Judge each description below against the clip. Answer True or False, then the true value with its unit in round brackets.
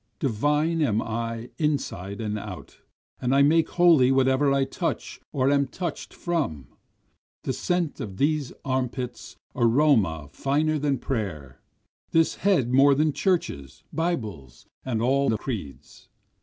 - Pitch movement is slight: False (5.3 semitones)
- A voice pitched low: True (130 Hz)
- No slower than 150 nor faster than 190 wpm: False (135 wpm)